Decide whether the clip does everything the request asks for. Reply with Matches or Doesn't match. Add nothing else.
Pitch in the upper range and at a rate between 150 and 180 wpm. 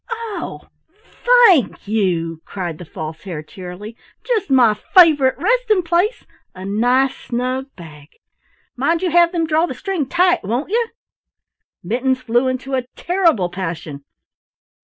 Doesn't match